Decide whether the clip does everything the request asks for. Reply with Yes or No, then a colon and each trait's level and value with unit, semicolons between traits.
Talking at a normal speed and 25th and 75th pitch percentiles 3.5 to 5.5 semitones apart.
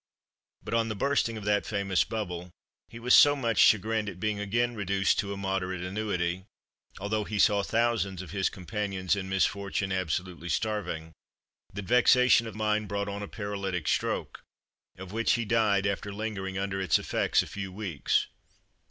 No: average, 170 wpm; narrow, 2.4 semitones